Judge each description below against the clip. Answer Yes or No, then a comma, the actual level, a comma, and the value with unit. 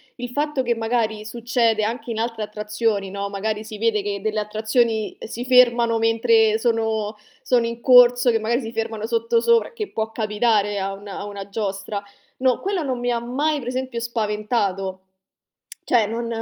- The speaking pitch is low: No, high, 225 Hz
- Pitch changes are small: Yes, narrow, 2.2 semitones